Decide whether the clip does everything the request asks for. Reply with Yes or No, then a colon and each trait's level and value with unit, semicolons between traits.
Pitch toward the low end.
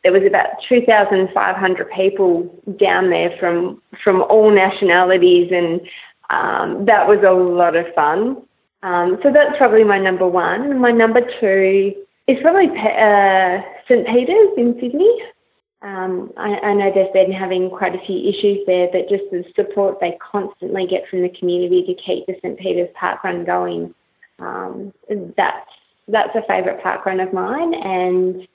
No: high, 190 Hz